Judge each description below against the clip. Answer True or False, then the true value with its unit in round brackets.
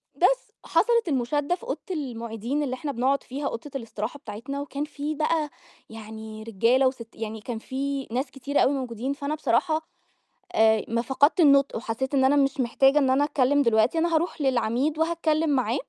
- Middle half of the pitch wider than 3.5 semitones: True (4.0 semitones)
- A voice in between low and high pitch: False (270 Hz)